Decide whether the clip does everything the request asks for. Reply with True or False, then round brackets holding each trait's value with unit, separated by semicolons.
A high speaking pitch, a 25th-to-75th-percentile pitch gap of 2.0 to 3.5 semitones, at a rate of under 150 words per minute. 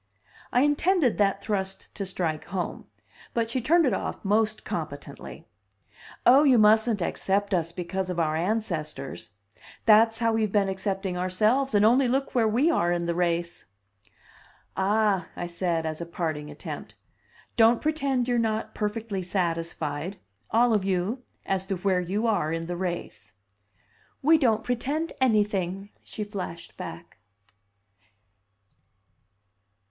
False (200 Hz; 4.6 semitones; 140 wpm)